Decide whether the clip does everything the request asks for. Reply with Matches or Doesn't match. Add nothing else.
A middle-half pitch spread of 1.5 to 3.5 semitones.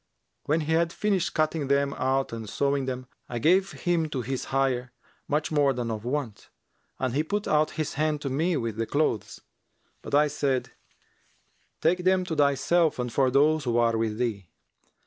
Doesn't match